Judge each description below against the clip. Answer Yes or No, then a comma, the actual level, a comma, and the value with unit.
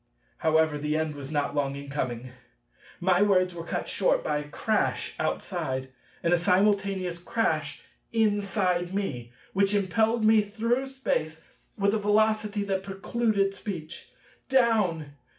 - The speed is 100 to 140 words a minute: Yes, slow, 135 wpm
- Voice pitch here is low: No, high, 190 Hz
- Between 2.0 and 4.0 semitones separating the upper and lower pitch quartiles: No, average, 5.0 semitones